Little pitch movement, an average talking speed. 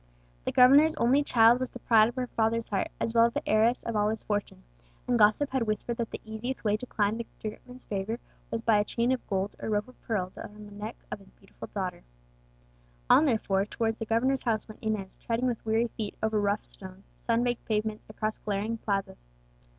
No: narrow, 2.3 semitones; fast, 220 wpm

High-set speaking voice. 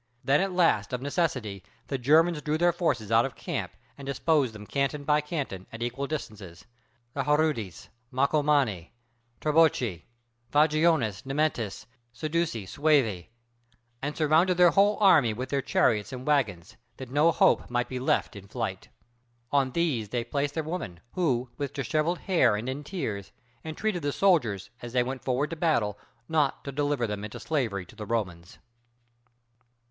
No: medium, 140 Hz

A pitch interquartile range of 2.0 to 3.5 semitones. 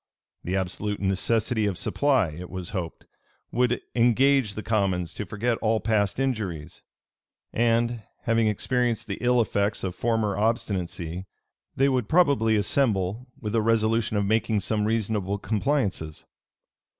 Yes: average, 3.2 semitones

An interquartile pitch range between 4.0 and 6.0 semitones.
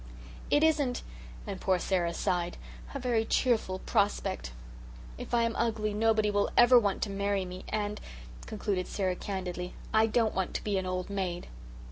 No: average, 3.2 semitones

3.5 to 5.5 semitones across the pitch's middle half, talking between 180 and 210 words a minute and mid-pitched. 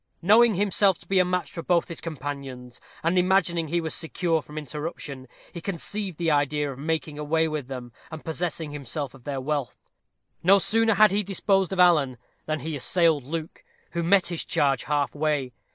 Yes: average, 3.8 semitones; average, 185 wpm; medium, 160 Hz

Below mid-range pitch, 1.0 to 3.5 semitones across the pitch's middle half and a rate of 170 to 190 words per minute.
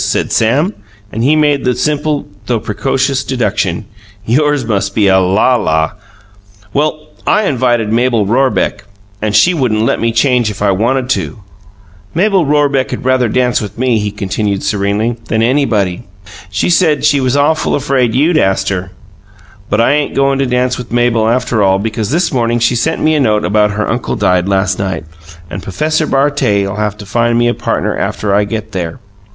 No: low, 120 Hz; average, 4.9 semitones; average, 180 wpm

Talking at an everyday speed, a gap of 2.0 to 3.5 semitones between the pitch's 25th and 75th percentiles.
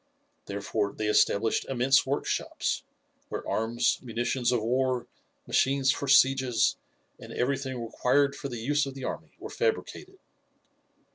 No: slow, 130 wpm; average, 2.8 semitones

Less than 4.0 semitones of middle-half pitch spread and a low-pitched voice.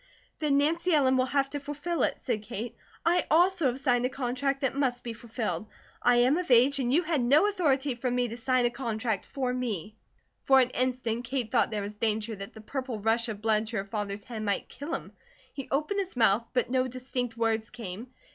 No: average, 3.4 semitones; very high, 250 Hz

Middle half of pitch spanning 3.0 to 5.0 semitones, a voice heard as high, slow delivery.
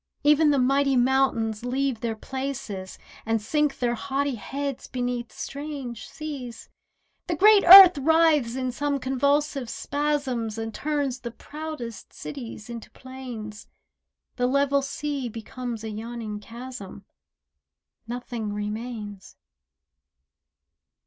Yes: average, 3.6 semitones; very high, 255 Hz; slow, 110 wpm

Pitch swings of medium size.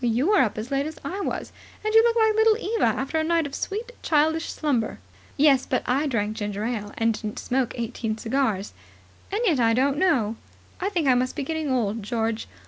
No: wide, 6.3 semitones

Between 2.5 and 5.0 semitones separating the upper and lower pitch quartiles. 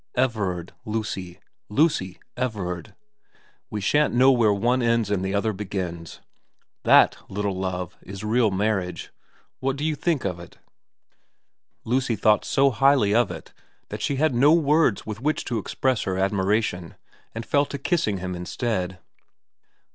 No: wide, 5.5 semitones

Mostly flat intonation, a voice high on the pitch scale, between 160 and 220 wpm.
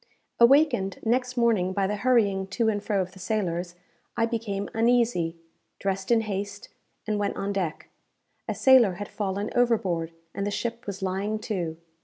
No: average, 3.3 semitones; high, 205 Hz; average, 165 wpm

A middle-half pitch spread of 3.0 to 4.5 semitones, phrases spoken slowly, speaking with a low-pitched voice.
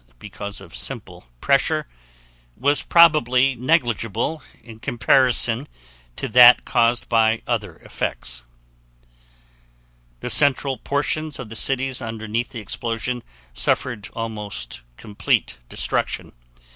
Yes: average, 3.3 semitones; slow, 100 wpm; low, 120 Hz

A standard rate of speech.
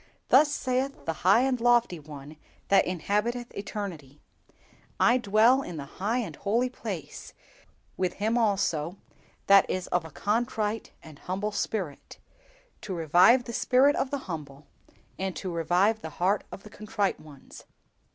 Yes: average, 150 wpm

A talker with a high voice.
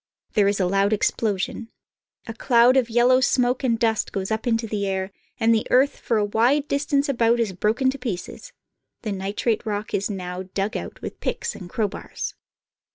Yes: high, 225 Hz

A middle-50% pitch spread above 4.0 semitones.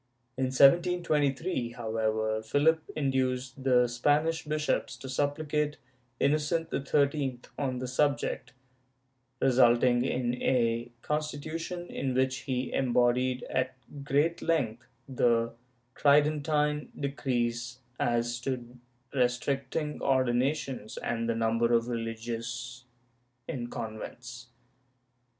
No: average, 3.4 semitones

